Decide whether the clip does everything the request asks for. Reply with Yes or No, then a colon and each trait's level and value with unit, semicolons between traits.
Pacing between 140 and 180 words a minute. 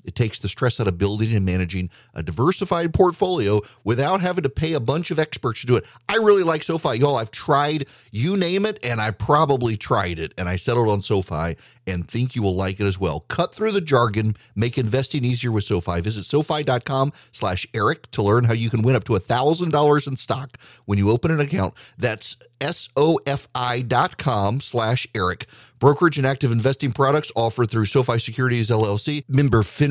No: average, 195 wpm